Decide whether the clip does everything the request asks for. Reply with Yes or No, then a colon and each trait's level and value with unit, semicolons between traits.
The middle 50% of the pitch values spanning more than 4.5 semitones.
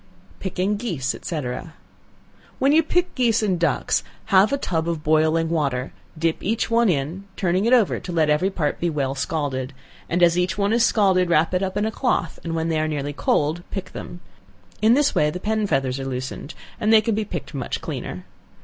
Yes: average, 5.3 semitones